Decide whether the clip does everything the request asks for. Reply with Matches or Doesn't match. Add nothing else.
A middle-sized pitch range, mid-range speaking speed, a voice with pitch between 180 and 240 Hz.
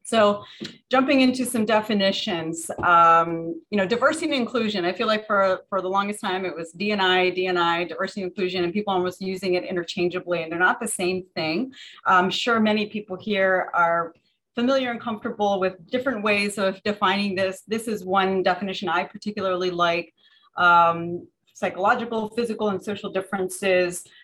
Matches